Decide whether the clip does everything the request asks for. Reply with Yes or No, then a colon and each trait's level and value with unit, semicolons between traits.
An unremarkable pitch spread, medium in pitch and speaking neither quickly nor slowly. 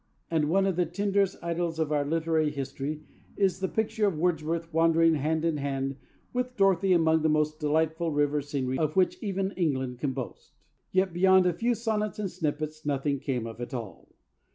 Yes: average, 4.2 semitones; medium, 160 Hz; average, 185 wpm